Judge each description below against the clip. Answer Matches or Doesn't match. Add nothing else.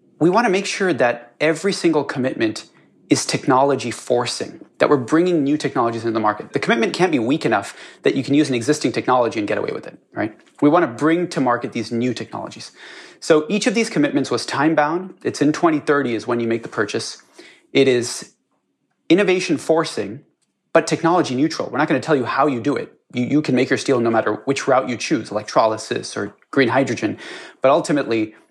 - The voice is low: Doesn't match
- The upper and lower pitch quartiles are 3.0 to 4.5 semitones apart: Doesn't match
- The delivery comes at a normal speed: Doesn't match